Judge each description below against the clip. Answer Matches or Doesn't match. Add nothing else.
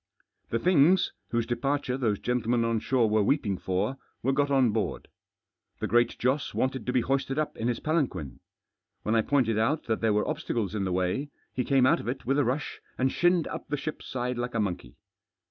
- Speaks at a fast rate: Matches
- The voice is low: Matches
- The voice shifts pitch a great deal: Doesn't match